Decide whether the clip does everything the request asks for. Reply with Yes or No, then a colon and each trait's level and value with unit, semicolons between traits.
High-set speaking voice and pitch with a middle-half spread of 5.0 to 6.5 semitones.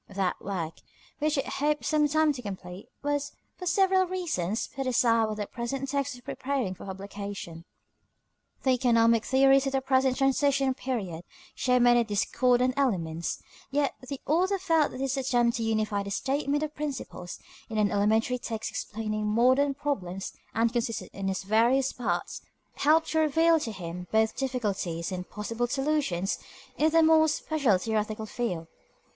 Yes: high, 245 Hz; average, 5.3 semitones